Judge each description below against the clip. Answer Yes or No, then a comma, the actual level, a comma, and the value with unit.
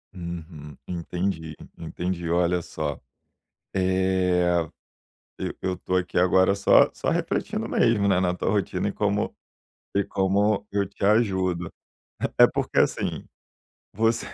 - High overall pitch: No, very low, 95 Hz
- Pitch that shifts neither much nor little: No, narrow, 2.2 semitones